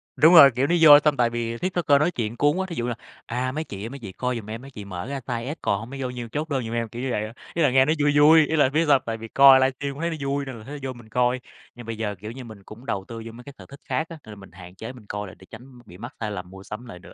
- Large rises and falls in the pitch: No, average, 4.2 semitones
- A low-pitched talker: Yes, low, 125 Hz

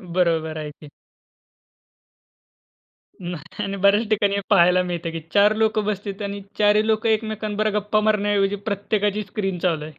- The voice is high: Yes, high, 200 Hz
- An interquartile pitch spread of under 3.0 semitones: Yes, narrow, 2.6 semitones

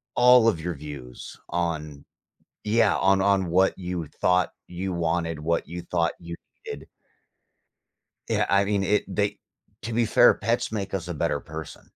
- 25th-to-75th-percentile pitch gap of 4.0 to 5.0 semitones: No, average, 3.2 semitones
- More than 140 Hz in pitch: No, very low, 90 Hz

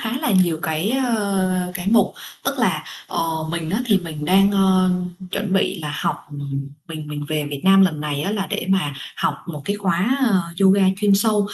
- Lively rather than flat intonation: No, average, 4.2 semitones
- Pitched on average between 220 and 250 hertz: No, medium, 185 Hz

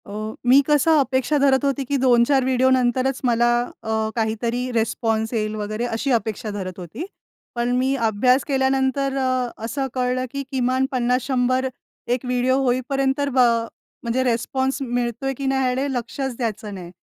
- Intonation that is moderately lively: No, narrow, 2.3 semitones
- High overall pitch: Yes, very high, 250 Hz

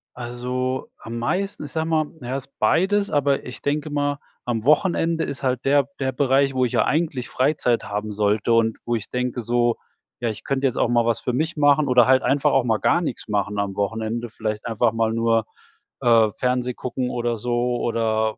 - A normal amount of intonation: Yes, average, 3.5 semitones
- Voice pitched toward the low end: Yes, low, 125 Hz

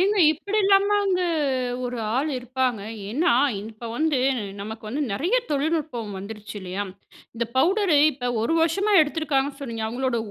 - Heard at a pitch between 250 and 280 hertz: Yes, very high, 275 Hz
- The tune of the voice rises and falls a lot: Yes, wide, 6.3 semitones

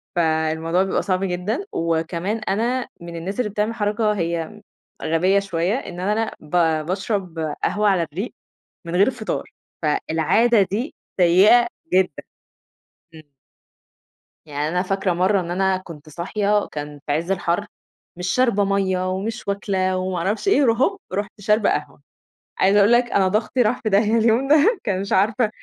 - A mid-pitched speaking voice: No, high, 195 Hz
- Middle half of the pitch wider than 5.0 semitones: No, average, 3.7 semitones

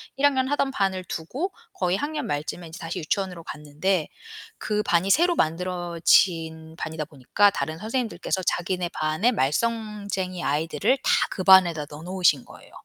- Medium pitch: Yes, medium, 180 Hz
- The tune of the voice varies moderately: Yes, average, 4.6 semitones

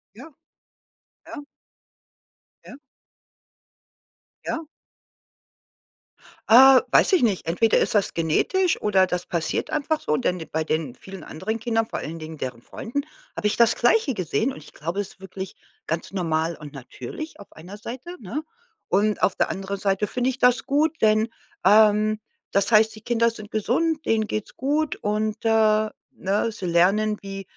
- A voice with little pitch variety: No, average, 4.4 semitones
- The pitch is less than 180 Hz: No, high, 215 Hz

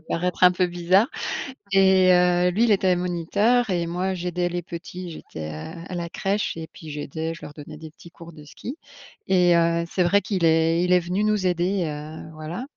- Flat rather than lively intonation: Yes, narrow, 2.1 semitones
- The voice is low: No, medium, 175 Hz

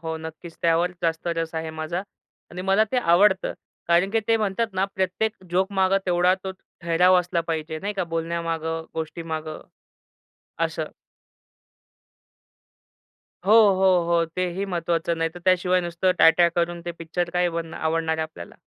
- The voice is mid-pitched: Yes, medium, 170 Hz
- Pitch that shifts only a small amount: Yes, narrow, 2.2 semitones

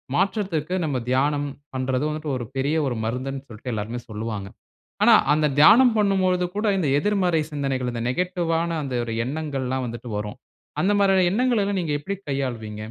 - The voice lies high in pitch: No, medium, 145 Hz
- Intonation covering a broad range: Yes, wide, 6.3 semitones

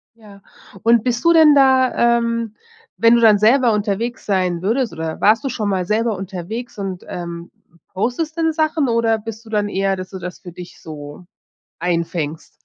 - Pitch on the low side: No, high, 215 Hz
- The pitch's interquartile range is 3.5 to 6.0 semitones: Yes, average, 4.4 semitones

